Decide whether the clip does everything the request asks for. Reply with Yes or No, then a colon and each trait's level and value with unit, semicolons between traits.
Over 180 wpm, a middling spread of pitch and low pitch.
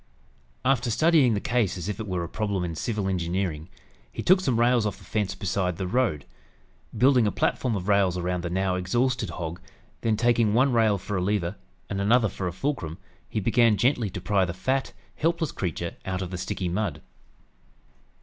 Yes: average, 195 wpm; average, 4.7 semitones; low, 100 Hz